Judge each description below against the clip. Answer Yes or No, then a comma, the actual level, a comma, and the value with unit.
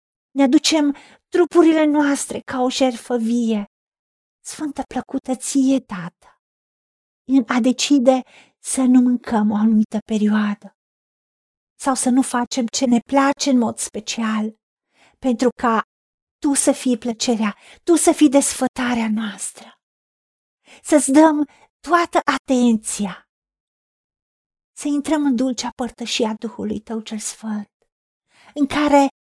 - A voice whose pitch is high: Yes, very high, 255 Hz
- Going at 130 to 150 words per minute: No, slow, 115 wpm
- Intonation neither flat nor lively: Yes, average, 3.9 semitones